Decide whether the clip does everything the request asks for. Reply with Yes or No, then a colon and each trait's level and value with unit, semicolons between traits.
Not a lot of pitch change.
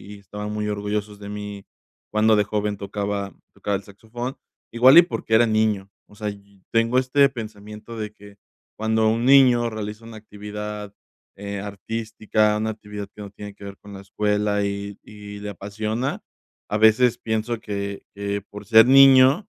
Yes: narrow, 1.6 semitones